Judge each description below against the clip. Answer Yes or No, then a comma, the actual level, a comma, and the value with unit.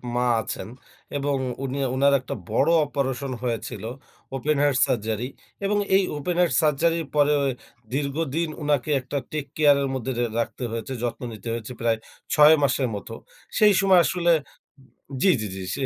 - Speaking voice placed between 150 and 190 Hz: No, medium, 140 Hz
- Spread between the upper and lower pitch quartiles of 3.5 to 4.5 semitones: Yes, average, 3.8 semitones